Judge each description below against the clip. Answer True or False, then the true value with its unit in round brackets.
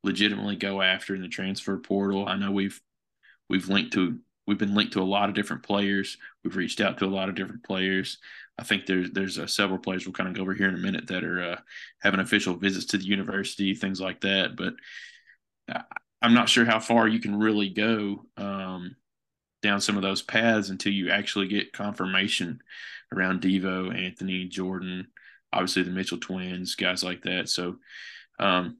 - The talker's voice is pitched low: True (95 Hz)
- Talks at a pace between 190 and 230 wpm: True (195 wpm)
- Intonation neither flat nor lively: False (1.4 semitones)